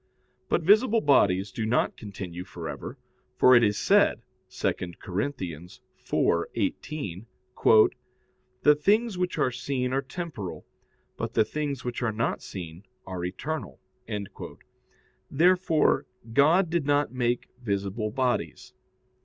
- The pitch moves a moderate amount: No, wide, 7.3 semitones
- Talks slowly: Yes, slow, 120 wpm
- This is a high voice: No, low, 125 Hz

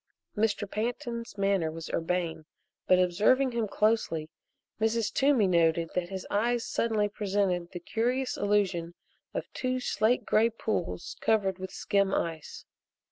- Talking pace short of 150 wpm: Yes, slow, 135 wpm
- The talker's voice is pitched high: Yes, high, 205 Hz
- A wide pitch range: No, average, 4.4 semitones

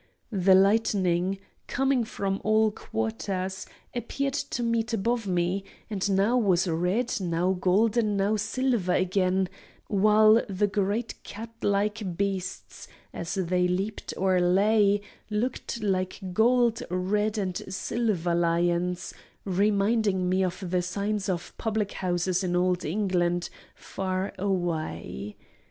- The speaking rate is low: Yes, slow, 120 wpm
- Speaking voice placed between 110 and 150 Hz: No, high, 195 Hz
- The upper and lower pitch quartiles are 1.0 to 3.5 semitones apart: Yes, average, 2.9 semitones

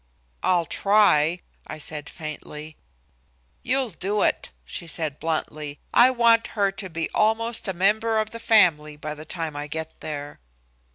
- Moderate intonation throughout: No, wide, 5.9 semitones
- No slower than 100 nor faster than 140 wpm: No, average, 155 wpm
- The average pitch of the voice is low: No, medium, 170 Hz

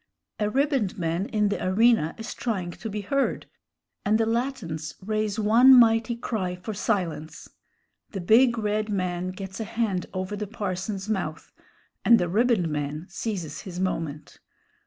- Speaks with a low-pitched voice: No, high, 205 Hz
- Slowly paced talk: No, average, 155 wpm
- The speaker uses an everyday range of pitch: Yes, average, 3.8 semitones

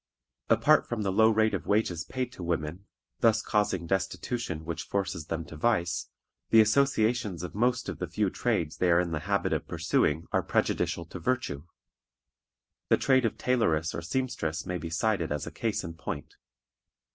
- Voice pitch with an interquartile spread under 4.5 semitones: No, average, 5.2 semitones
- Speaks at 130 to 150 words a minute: No, average, 180 wpm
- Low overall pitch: Yes, very low, 95 Hz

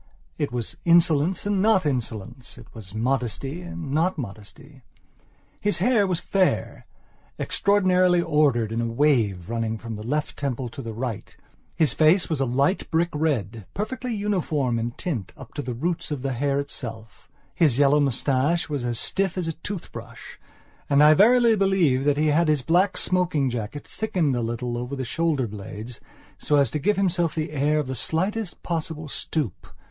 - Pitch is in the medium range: Yes, medium, 145 Hz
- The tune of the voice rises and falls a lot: Yes, wide, 6.1 semitones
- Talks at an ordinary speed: Yes, average, 175 wpm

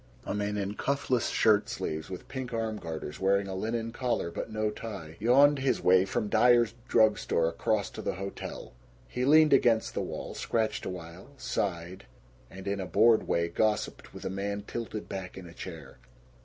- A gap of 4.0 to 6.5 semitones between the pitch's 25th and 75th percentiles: No, average, 3.6 semitones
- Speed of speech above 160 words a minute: Yes, average, 185 wpm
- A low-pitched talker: Yes, low, 105 Hz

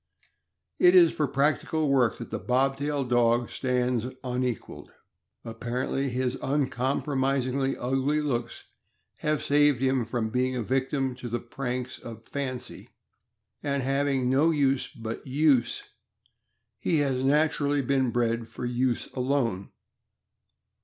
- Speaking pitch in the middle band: No, low, 130 Hz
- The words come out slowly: Yes, slow, 125 wpm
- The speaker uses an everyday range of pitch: No, narrow, 2.3 semitones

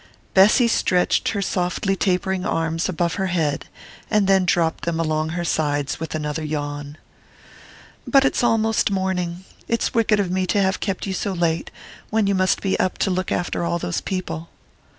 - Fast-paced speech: No, average, 175 wpm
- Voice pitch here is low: No, medium, 180 Hz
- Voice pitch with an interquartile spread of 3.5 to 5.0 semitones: No, average, 3.1 semitones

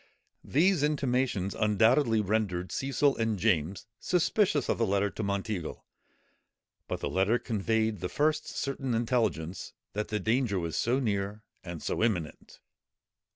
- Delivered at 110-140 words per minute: Yes, slow, 135 wpm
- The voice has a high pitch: No, low, 110 Hz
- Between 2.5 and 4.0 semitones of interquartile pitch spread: No, average, 4.8 semitones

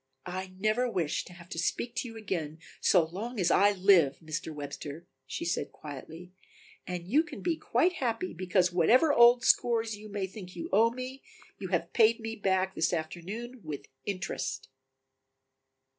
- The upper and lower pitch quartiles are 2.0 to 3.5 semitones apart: No, average, 5.1 semitones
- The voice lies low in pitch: No, high, 190 Hz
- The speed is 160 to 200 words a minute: Yes, average, 170 wpm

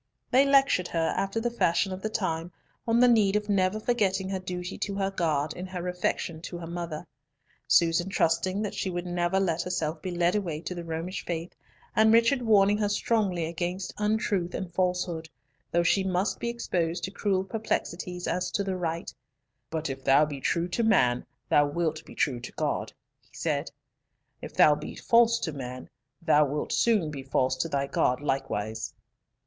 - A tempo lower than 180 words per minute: No, average, 185 wpm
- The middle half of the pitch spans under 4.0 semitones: Yes, average, 3.6 semitones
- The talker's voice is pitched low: No, medium, 180 Hz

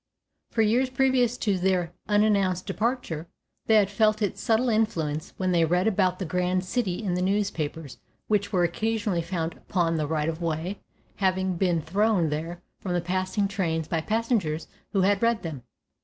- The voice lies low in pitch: No, medium, 185 Hz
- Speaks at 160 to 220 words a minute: Yes, average, 170 wpm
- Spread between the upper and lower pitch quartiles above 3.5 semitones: Yes, average, 4.1 semitones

